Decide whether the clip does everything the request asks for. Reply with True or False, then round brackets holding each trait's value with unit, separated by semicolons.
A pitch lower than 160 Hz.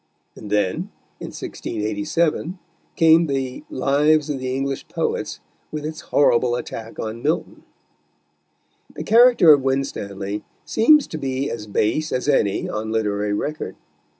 True (135 Hz)